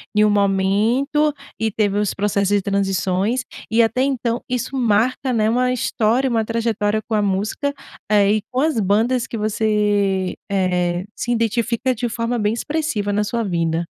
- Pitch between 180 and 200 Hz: No, high, 215 Hz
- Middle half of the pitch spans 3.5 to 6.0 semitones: No, average, 3.1 semitones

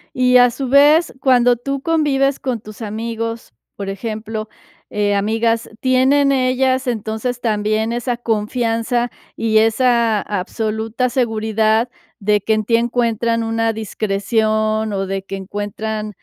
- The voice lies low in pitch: No, high, 225 Hz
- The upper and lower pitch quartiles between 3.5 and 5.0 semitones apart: No, narrow, 2.4 semitones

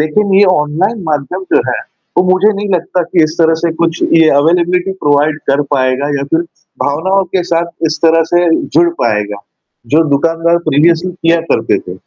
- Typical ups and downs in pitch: Yes, average, 3.3 semitones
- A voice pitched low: No, medium, 165 Hz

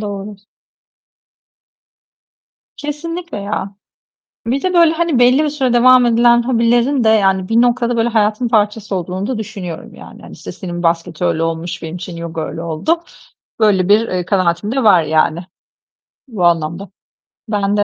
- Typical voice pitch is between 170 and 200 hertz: No, high, 210 Hz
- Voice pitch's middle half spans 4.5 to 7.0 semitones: Yes, wide, 5.4 semitones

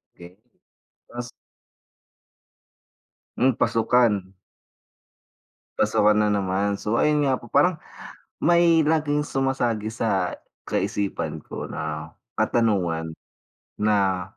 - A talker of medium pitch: No, low, 110 Hz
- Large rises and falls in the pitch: Yes, wide, 5.7 semitones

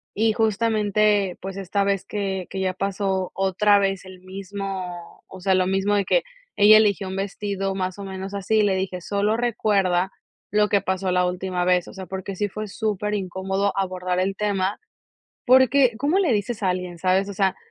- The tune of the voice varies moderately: No, narrow, 1.8 semitones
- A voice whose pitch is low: No, high, 195 Hz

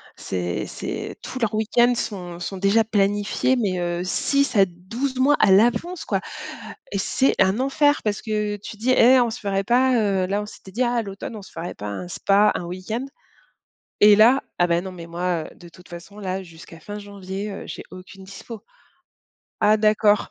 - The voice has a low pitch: No, high, 205 Hz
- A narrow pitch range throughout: No, average, 3.7 semitones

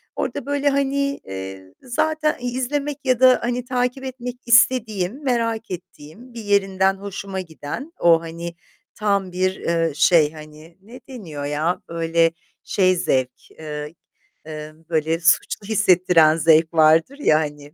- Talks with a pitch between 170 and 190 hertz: Yes, medium, 185 Hz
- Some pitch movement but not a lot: No, wide, 7.6 semitones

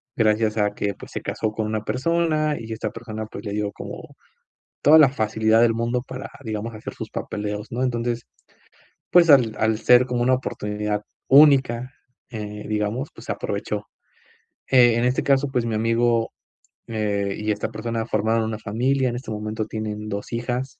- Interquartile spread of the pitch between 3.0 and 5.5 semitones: No, narrow, 2.6 semitones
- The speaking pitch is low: Yes, low, 115 Hz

